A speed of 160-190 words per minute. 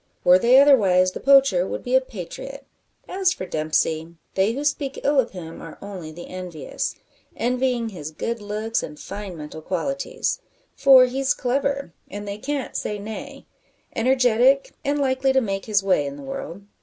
Yes: average, 170 wpm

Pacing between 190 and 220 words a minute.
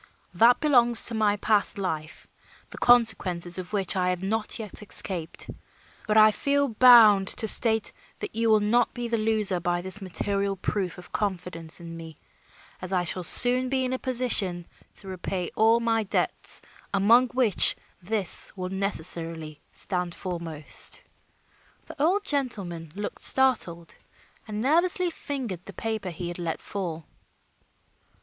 No: average, 150 wpm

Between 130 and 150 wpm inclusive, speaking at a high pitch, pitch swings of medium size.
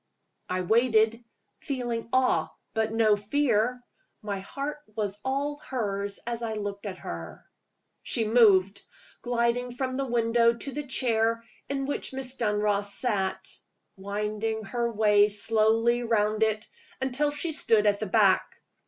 Yes: slow, 135 wpm; high, 225 Hz; average, 3.0 semitones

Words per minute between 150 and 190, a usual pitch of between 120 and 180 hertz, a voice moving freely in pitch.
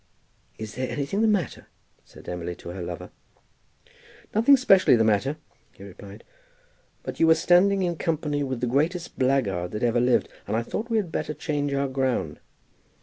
Yes: average, 175 wpm; low, 135 Hz; wide, 7.8 semitones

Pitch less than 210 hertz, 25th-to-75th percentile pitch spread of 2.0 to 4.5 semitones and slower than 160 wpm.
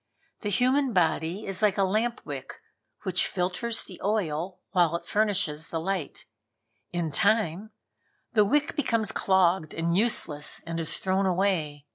Yes: high, 190 Hz; average, 4.2 semitones; average, 140 wpm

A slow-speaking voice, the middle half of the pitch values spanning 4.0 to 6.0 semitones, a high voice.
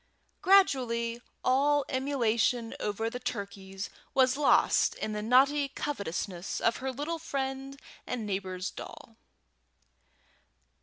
Yes: slow, 105 wpm; average, 4.5 semitones; very high, 250 Hz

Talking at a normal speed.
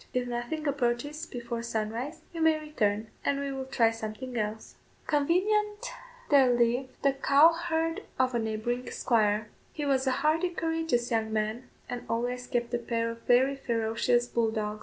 Yes: average, 165 wpm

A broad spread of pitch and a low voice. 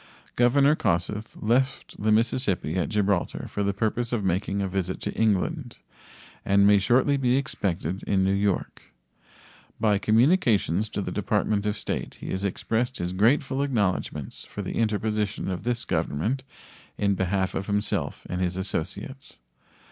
No: average, 4.0 semitones; low, 105 Hz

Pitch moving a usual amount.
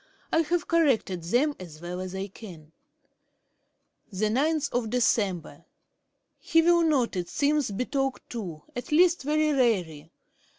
No: wide, 8.4 semitones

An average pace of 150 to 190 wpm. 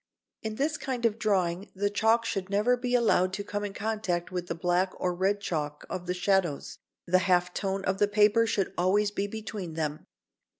No: average, 200 wpm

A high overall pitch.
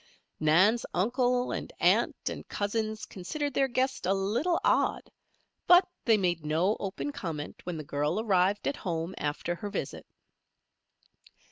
Yes: high, 200 Hz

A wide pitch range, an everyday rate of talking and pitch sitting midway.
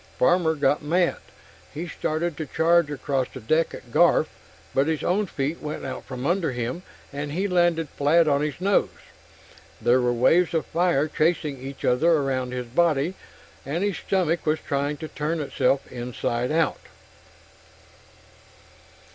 No: average, 3.8 semitones; average, 155 wpm; medium, 155 Hz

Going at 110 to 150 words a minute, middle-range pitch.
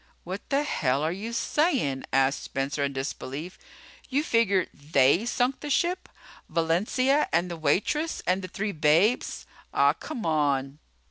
Yes: average, 145 wpm; medium, 180 Hz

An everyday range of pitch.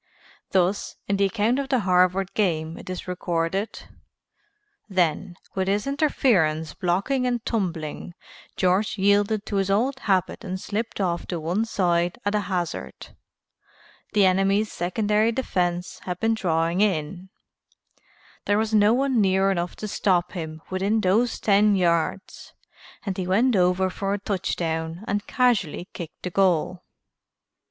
Yes: average, 3.0 semitones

